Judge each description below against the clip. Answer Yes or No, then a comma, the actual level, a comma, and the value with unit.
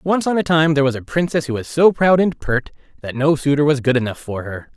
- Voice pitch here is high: No, medium, 145 Hz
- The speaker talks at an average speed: No, fast, 275 wpm